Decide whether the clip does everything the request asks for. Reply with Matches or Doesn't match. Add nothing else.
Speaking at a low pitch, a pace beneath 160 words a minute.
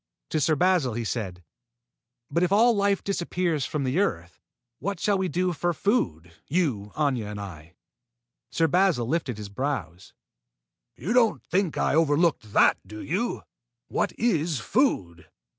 Doesn't match